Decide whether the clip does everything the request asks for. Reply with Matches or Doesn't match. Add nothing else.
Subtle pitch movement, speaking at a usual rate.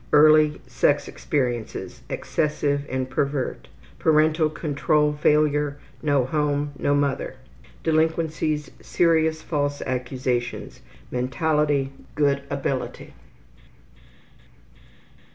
Doesn't match